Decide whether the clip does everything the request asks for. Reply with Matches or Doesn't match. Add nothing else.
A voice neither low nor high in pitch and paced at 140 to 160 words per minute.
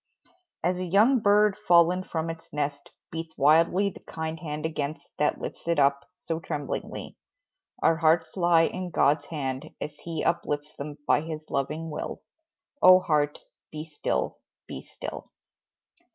Matches